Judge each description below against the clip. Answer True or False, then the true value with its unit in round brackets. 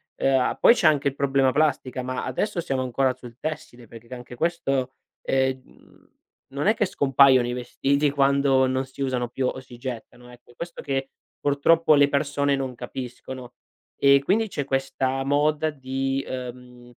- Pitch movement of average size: False (1.9 semitones)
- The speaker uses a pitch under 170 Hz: True (135 Hz)